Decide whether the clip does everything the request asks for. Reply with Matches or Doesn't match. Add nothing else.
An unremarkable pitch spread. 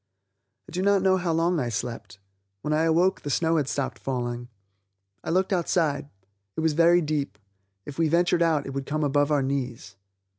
Matches